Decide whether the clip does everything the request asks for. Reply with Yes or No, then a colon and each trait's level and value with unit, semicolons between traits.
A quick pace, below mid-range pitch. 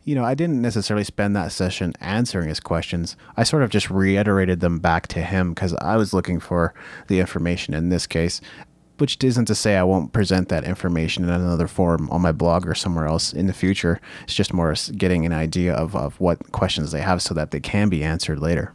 Yes: fast, 225 wpm; very low, 90 Hz